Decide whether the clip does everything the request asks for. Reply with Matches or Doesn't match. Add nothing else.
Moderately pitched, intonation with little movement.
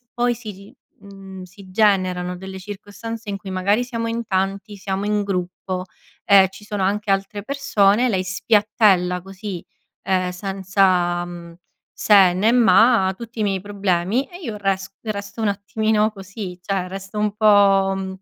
Doesn't match